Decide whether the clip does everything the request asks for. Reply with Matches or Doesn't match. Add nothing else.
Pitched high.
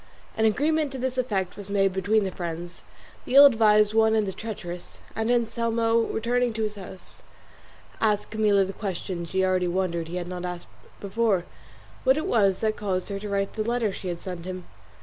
Matches